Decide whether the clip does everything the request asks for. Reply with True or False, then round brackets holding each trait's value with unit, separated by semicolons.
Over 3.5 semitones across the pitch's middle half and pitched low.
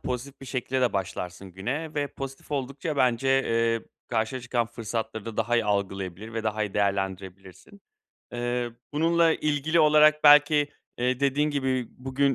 True (4.4 semitones; 125 Hz)